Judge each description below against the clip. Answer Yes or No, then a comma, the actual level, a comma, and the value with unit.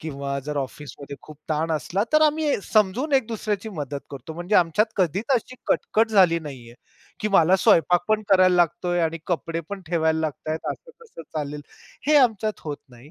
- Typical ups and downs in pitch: No, wide, 5.8 semitones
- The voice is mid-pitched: Yes, medium, 175 Hz